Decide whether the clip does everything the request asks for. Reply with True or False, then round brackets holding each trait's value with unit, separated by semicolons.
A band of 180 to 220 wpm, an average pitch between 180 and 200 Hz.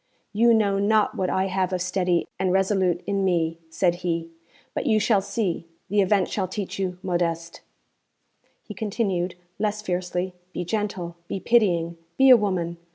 False (160 wpm; 190 Hz)